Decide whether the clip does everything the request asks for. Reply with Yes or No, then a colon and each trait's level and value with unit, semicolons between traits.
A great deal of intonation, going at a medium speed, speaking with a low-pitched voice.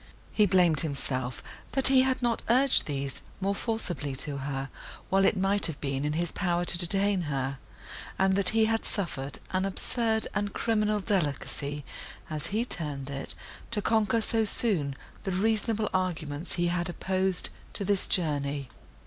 No: wide, 6.3 semitones; average, 160 wpm; medium, 185 Hz